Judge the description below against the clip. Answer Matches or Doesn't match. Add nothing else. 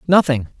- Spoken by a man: Matches